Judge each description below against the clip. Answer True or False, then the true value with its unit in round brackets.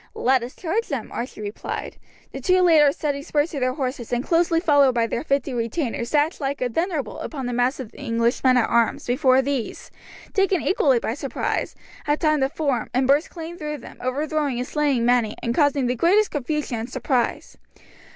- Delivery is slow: False (200 wpm)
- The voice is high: True (275 Hz)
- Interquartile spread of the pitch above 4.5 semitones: False (3.8 semitones)